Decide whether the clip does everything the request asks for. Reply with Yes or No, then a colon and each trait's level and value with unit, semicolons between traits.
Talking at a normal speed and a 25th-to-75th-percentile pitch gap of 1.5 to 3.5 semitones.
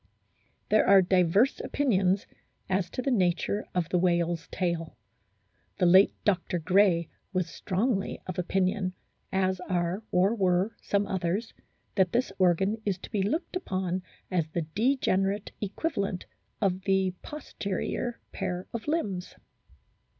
No: slow, 130 wpm; narrow, 2.4 semitones